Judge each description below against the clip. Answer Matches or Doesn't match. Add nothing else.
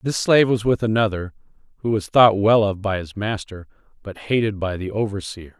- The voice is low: Matches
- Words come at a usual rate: Matches